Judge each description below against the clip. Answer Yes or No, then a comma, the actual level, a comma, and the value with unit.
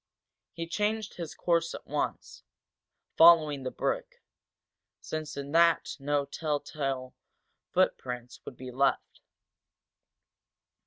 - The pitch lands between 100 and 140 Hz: No, medium, 150 Hz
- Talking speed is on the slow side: Yes, slow, 100 wpm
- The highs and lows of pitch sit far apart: No, average, 3.6 semitones